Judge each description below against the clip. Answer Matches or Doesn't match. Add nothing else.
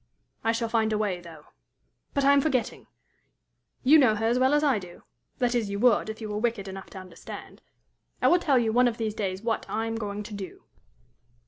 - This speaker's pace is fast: Matches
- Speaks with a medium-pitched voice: Doesn't match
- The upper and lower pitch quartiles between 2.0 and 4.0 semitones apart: Matches